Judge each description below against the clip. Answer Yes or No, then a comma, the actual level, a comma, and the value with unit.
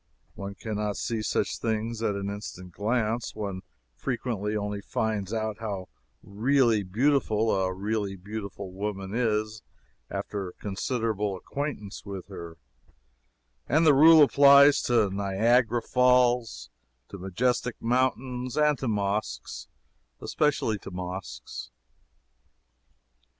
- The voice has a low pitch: Yes, low, 110 Hz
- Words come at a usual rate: No, slow, 115 wpm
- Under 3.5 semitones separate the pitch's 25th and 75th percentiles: No, average, 3.8 semitones